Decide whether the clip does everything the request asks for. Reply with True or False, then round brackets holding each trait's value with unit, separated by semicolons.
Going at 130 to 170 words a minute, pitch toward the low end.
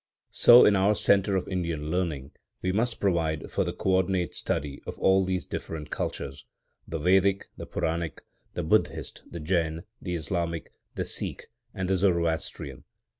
True (155 wpm; 90 Hz)